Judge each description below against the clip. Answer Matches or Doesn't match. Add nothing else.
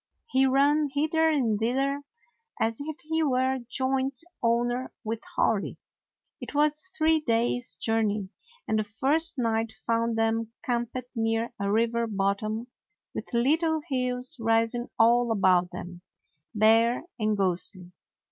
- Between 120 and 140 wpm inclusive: Matches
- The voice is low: Doesn't match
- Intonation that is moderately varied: Matches